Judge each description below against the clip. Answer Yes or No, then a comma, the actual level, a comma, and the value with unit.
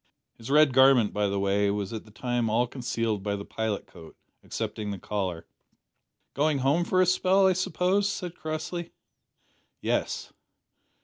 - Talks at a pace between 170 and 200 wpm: No, average, 160 wpm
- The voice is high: No, low, 120 Hz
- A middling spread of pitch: No, wide, 8.0 semitones